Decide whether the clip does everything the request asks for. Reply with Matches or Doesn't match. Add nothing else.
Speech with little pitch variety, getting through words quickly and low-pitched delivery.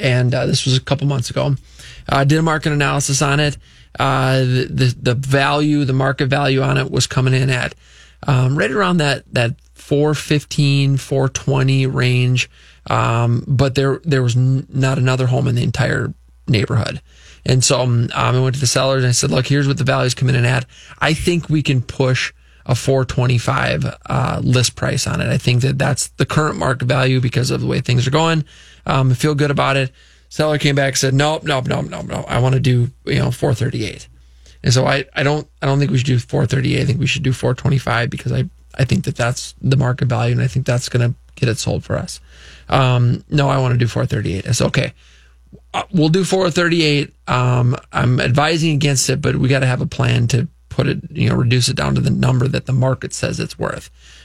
Matches